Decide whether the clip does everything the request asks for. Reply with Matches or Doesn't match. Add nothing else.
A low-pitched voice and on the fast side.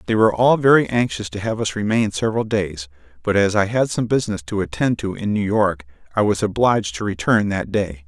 Matches